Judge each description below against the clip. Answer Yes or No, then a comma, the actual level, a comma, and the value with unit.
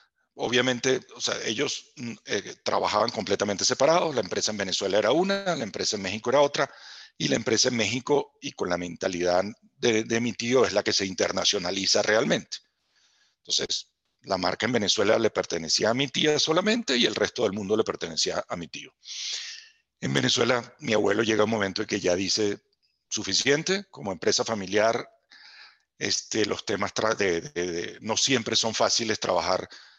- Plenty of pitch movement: Yes, wide, 5.7 semitones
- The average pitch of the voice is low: Yes, low, 115 Hz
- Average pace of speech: Yes, average, 175 wpm